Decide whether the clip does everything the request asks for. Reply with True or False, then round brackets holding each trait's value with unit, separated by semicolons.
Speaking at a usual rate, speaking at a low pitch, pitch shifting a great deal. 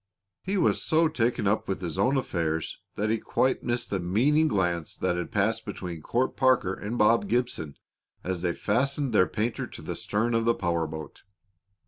True (180 wpm; 105 Hz; 5.7 semitones)